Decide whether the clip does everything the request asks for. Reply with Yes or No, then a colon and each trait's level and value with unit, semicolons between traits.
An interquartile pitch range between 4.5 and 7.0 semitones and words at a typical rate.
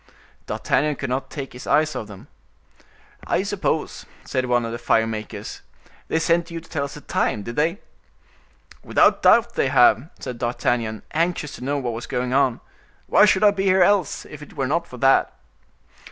Yes: wide, 5.4 semitones; average, 190 wpm